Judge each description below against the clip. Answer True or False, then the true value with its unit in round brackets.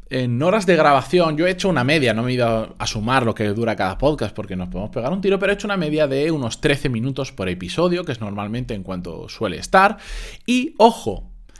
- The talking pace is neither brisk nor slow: False (240 wpm)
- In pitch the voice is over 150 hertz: False (130 Hz)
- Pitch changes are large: True (8.6 semitones)